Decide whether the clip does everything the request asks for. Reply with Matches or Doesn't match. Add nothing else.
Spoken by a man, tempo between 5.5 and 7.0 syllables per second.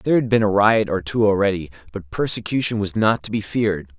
Matches